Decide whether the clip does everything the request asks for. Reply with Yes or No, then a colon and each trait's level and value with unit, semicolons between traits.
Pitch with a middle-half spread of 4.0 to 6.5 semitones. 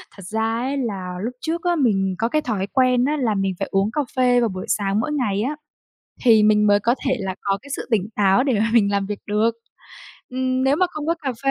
Yes: average, 4.5 semitones